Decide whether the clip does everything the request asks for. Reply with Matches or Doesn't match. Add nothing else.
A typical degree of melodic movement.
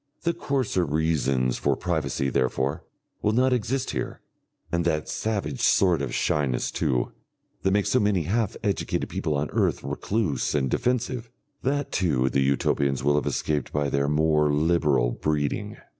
Doesn't match